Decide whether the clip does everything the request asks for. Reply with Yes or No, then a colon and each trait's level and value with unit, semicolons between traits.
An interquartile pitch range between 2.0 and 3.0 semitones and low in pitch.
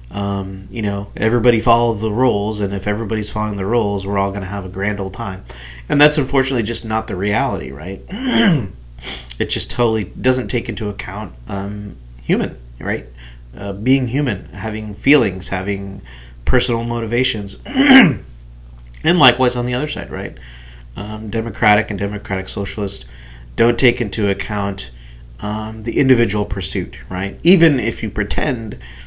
No: average, 3.8 semitones; low, 105 Hz